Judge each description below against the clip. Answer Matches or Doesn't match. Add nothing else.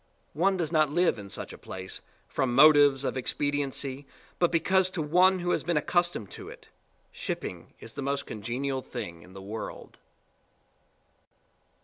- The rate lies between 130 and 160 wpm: Matches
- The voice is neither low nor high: Matches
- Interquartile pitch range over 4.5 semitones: Matches